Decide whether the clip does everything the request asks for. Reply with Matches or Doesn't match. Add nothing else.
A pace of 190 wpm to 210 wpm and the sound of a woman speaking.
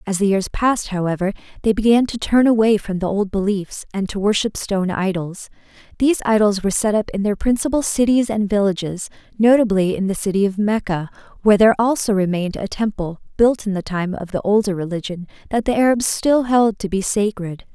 Matches